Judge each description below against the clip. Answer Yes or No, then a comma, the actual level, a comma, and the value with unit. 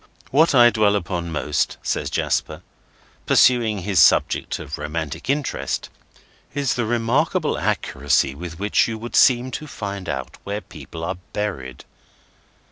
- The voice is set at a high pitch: No, low, 105 Hz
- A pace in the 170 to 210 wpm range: No, slow, 135 wpm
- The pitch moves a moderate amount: No, wide, 6.2 semitones